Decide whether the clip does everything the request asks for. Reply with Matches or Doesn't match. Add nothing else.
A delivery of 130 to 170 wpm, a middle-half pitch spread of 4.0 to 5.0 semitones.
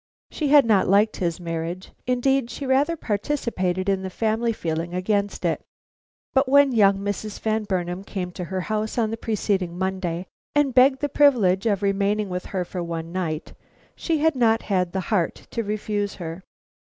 Doesn't match